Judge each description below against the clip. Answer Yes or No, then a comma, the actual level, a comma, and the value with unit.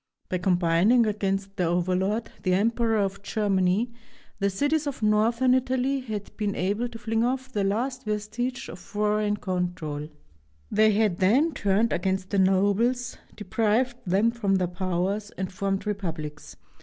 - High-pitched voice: Yes, high, 205 Hz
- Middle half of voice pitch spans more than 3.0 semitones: Yes, average, 3.6 semitones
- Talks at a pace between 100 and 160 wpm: Yes, average, 145 wpm